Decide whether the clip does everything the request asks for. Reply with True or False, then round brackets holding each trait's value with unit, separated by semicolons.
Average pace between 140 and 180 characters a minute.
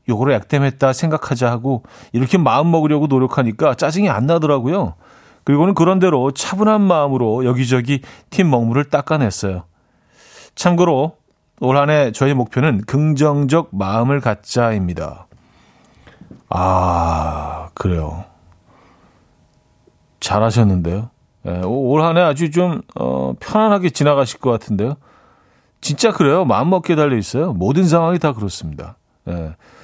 False (285 characters per minute)